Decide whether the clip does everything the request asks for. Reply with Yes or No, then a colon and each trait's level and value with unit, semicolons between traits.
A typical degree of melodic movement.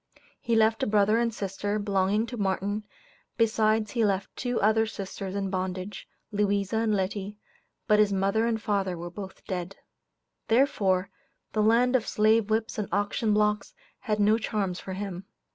No: narrow, 2.1 semitones